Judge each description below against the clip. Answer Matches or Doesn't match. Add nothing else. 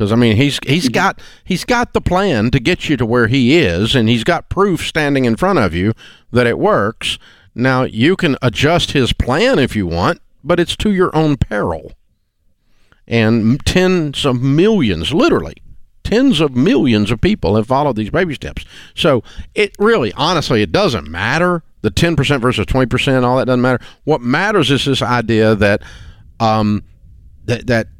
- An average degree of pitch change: Doesn't match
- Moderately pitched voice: Doesn't match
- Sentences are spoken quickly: Doesn't match